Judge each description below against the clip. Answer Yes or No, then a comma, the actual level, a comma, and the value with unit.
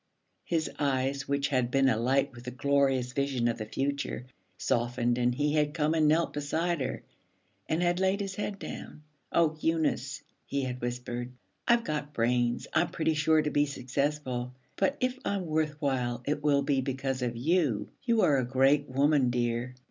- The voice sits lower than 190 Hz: Yes, medium, 140 Hz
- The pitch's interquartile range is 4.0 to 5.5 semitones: No, average, 3.6 semitones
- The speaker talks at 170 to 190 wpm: Yes, average, 180 wpm